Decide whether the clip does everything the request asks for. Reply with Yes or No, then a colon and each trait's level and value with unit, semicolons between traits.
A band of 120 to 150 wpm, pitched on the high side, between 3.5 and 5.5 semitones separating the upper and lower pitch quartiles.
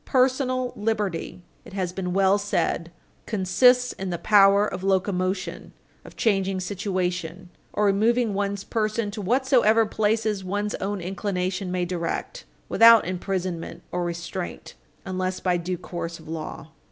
No: slow, 135 wpm; high, 195 Hz; average, 2.8 semitones